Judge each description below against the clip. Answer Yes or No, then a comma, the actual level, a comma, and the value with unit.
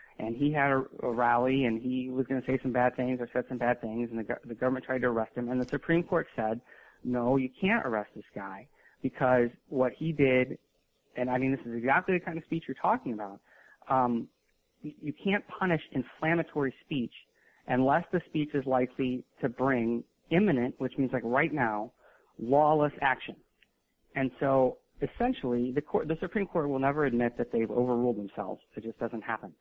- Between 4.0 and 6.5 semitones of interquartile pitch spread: No, average, 3.3 semitones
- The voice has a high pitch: No, low, 130 Hz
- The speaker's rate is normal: Yes, average, 190 wpm